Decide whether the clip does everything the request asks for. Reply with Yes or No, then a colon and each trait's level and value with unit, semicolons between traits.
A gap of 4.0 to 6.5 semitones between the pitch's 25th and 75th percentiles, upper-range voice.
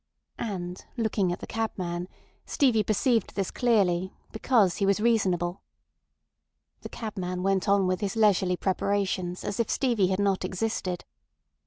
No: average, 3.3 semitones; high, 195 Hz